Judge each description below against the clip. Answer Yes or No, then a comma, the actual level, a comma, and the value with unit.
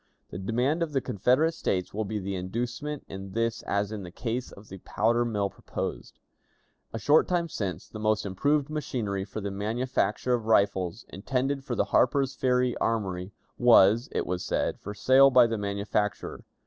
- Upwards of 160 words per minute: Yes, average, 175 wpm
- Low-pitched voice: Yes, low, 110 Hz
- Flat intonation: No, average, 4.3 semitones